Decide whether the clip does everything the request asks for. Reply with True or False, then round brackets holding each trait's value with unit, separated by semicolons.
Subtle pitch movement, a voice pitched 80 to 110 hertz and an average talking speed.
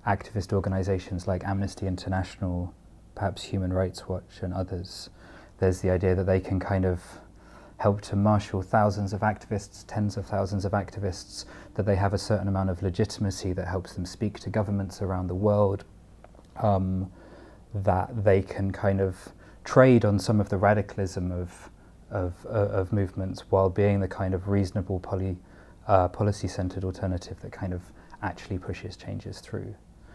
True (1.6 semitones; 95 Hz; 160 wpm)